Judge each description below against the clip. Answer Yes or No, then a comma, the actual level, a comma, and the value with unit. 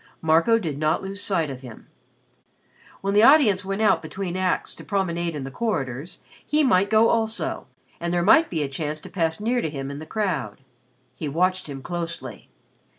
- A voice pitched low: No, medium, 175 Hz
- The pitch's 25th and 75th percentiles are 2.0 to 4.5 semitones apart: No, average, 4.9 semitones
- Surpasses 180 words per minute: Yes, average, 190 wpm